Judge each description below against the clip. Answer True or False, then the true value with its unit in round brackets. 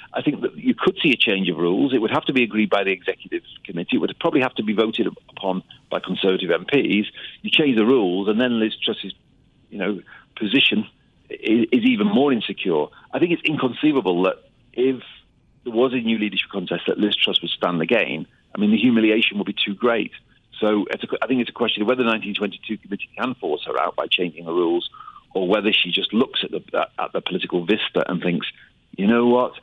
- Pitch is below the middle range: True (115 Hz)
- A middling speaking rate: False (225 wpm)